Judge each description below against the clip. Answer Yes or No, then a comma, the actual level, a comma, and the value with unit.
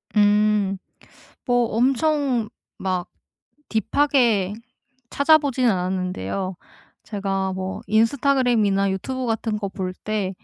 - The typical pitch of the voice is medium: No, high, 210 Hz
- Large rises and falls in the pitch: No, average, 4.5 semitones